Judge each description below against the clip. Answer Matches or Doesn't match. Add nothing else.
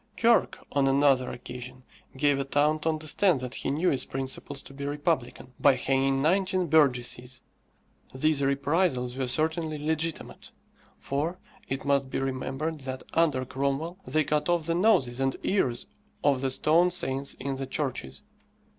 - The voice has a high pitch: Doesn't match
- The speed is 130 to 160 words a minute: Matches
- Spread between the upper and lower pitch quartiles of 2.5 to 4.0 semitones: Matches